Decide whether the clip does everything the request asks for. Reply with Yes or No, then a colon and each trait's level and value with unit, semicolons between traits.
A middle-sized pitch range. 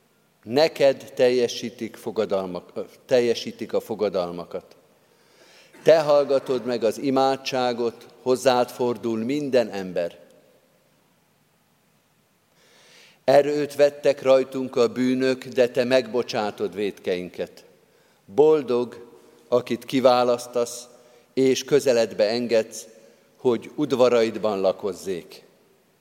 No: narrow, 2.2 semitones